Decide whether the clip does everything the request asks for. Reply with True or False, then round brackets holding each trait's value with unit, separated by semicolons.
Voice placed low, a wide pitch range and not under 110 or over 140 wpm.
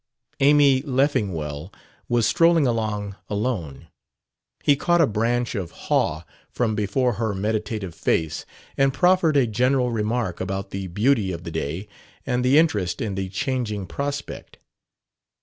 True (110 Hz; 5.7 semitones; 135 wpm)